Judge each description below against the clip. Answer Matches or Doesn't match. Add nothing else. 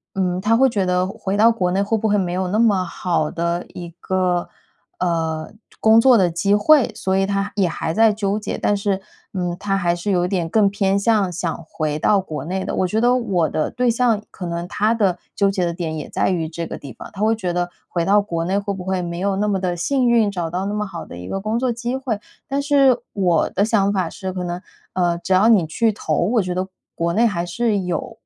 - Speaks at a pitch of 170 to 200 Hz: Matches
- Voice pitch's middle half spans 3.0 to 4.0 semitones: Matches